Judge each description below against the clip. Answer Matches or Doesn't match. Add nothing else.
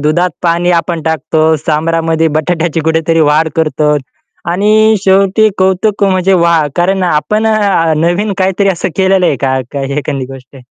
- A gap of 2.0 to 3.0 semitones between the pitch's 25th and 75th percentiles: Doesn't match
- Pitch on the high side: Doesn't match